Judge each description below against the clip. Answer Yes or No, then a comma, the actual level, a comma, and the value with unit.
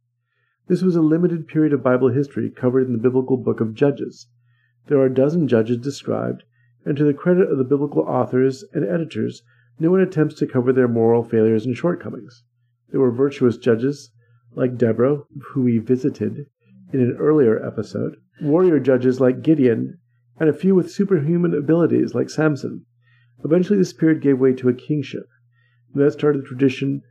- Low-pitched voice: Yes, low, 130 Hz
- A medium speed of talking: Yes, average, 175 wpm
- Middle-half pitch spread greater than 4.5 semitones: No, average, 3.6 semitones